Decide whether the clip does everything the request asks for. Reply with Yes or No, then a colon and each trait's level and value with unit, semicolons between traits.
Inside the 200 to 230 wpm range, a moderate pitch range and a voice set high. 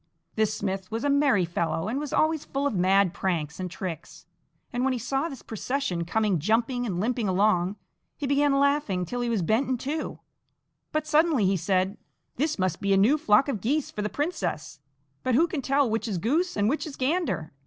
No: fast, 205 wpm; wide, 6.7 semitones; high, 225 Hz